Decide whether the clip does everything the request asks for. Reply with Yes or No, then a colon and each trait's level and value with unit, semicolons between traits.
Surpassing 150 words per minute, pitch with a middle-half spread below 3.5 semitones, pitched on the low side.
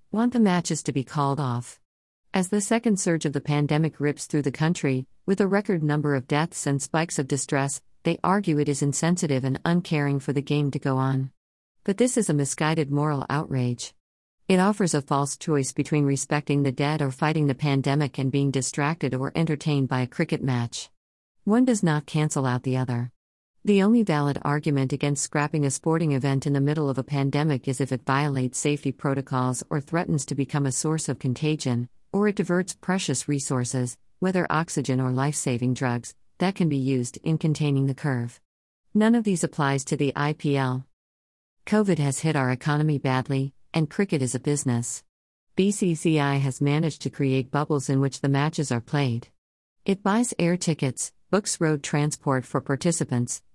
No: average, 185 wpm; average, 3.1 semitones; medium, 145 Hz